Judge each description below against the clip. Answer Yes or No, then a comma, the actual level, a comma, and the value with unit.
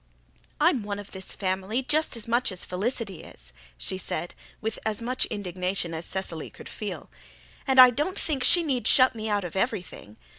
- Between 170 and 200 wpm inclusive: Yes, average, 185 wpm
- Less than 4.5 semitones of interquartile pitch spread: No, average, 5.1 semitones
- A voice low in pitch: No, high, 205 Hz